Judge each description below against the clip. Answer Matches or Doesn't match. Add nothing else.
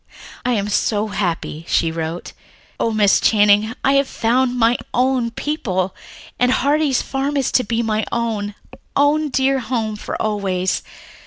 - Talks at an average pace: Matches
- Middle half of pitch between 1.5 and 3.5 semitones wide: Doesn't match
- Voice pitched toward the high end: Matches